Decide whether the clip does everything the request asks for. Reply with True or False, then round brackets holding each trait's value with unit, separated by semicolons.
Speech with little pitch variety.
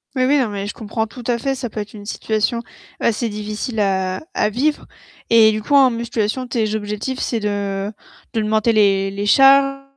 False (3.1 semitones)